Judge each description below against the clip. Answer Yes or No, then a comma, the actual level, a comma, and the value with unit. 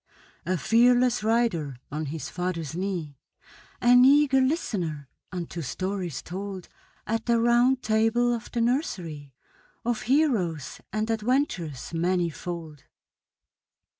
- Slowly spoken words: Yes, slow, 105 wpm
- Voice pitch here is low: No, high, 200 Hz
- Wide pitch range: Yes, wide, 6.4 semitones